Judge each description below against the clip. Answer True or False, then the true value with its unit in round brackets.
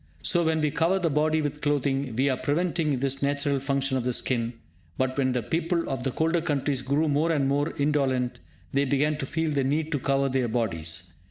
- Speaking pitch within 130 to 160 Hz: True (140 Hz)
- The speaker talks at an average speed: False (210 wpm)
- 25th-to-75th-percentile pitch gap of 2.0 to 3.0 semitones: True (2.7 semitones)